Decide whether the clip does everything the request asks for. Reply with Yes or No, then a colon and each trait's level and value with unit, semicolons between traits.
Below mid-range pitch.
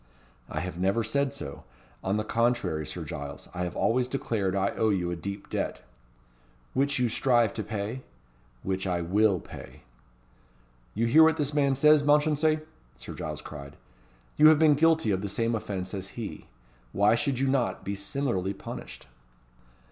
Yes: low, 110 Hz